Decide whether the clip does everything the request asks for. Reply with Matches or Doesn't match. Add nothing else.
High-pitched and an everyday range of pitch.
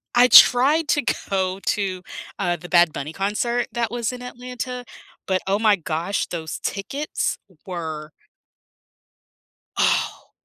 Doesn't match